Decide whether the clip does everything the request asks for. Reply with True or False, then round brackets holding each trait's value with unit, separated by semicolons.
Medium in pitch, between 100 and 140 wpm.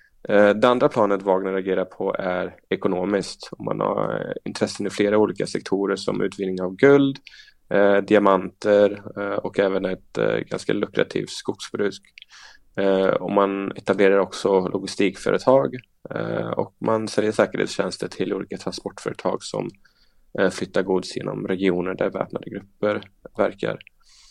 False (100 Hz; 130 wpm)